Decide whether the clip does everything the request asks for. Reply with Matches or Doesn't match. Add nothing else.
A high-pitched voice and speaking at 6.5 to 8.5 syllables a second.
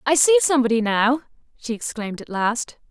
Doesn't match